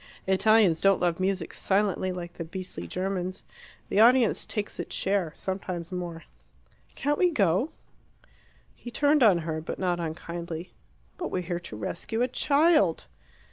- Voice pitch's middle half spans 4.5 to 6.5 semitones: No, average, 4.0 semitones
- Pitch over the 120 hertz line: Yes, medium, 185 Hz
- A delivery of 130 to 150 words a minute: Yes, average, 145 wpm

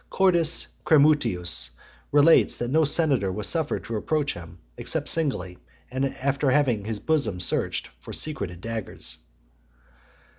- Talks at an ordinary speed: No, slow, 125 wpm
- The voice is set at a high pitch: No, low, 135 Hz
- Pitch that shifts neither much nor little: No, wide, 8.2 semitones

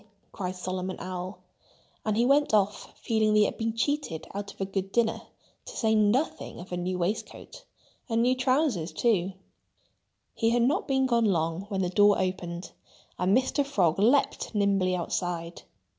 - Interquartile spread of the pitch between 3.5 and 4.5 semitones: Yes, average, 4.2 semitones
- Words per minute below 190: Yes, average, 160 wpm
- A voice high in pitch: Yes, high, 205 Hz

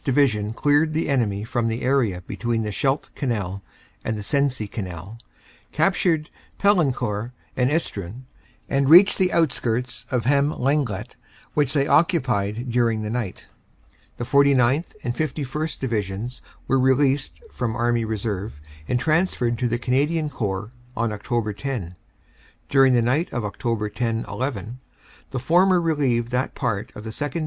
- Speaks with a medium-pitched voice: No, low, 125 Hz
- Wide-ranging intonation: No, average, 4.2 semitones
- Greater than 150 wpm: No, average, 145 wpm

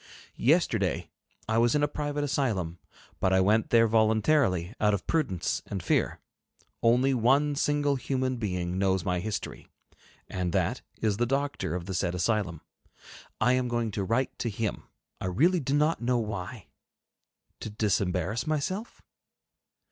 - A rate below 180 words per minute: Yes, average, 150 wpm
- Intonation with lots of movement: Yes, wide, 6.3 semitones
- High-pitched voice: No, low, 115 Hz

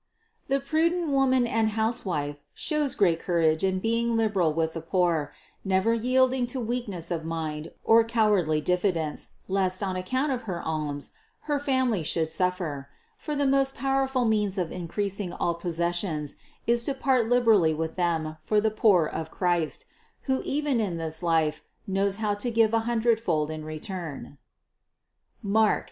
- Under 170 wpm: Yes, average, 155 wpm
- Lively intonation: Yes, wide, 6.3 semitones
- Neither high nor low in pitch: No, high, 195 Hz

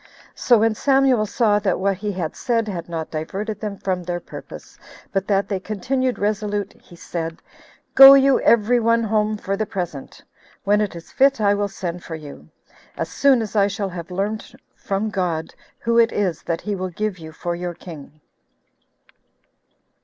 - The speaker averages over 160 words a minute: Yes, average, 180 wpm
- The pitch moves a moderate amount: Yes, average, 3.6 semitones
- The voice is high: Yes, high, 200 Hz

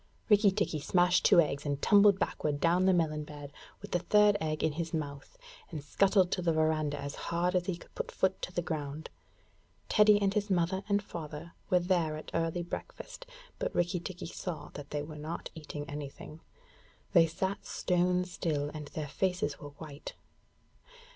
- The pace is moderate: Yes, average, 180 wpm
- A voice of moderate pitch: Yes, medium, 170 Hz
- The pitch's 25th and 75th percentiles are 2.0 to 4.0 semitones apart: Yes, average, 3.6 semitones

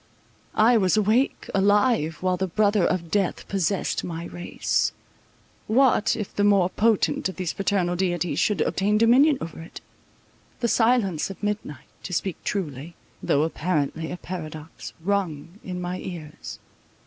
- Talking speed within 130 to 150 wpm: Yes, average, 145 wpm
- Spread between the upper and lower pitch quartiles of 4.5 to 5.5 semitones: No, average, 3.8 semitones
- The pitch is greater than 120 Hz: Yes, medium, 185 Hz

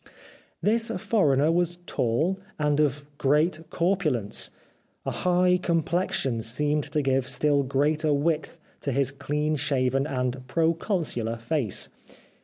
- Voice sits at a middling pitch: Yes, medium, 150 Hz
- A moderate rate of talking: No, slow, 125 wpm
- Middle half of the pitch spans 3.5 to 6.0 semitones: Yes, average, 3.9 semitones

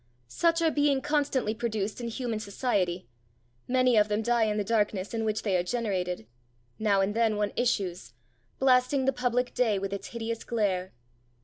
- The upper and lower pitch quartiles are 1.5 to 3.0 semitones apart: No, average, 3.6 semitones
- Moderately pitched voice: No, high, 220 Hz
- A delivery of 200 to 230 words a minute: No, average, 175 wpm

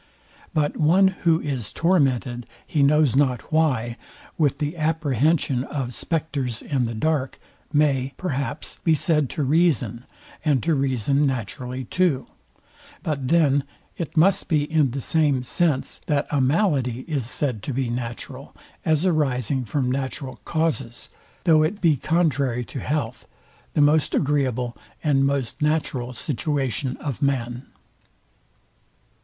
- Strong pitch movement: No, average, 3.5 semitones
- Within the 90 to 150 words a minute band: Yes, slow, 135 wpm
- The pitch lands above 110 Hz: Yes, medium, 140 Hz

